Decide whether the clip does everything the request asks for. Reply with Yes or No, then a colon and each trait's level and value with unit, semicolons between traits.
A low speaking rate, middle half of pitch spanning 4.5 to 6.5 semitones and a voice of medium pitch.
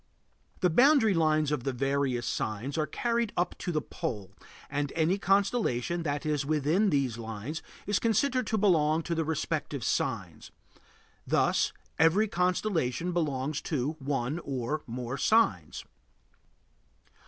Yes: slow, 130 wpm; average, 5.0 semitones; medium, 155 Hz